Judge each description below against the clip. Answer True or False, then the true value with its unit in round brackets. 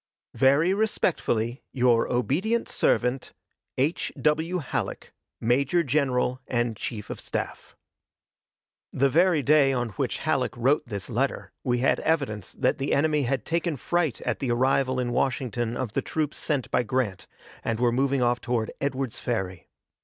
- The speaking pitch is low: True (130 Hz)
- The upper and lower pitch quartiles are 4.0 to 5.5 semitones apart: False (3.6 semitones)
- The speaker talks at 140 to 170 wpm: True (150 wpm)